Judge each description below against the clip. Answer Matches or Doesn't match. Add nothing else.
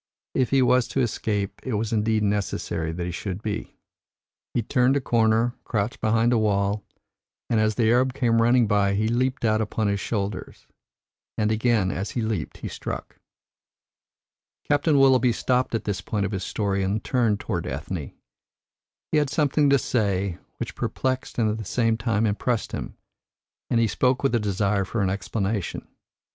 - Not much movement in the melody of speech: Doesn't match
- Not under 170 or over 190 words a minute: Matches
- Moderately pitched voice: Doesn't match